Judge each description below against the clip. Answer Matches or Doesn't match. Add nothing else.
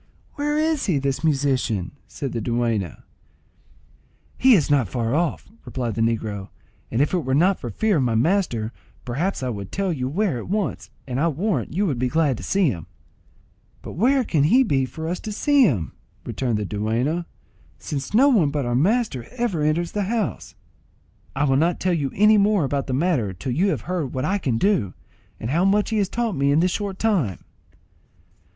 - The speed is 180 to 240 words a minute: Matches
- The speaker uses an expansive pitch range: Matches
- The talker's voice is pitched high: Doesn't match